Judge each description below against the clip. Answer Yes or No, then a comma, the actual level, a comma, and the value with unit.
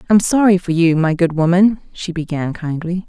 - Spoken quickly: No, average, 195 wpm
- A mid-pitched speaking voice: Yes, medium, 175 Hz